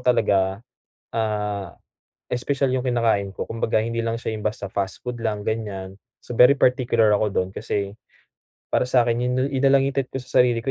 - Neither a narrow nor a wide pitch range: Yes, average, 3.4 semitones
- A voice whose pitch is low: Yes, low, 115 Hz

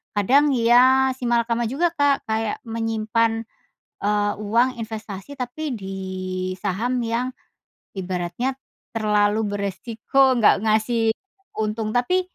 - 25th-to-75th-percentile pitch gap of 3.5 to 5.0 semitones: No, average, 3.0 semitones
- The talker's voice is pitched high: Yes, high, 225 Hz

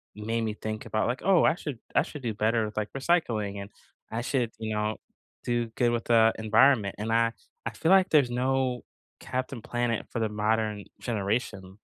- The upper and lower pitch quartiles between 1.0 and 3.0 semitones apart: Yes, narrow, 2.6 semitones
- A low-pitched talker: Yes, low, 115 Hz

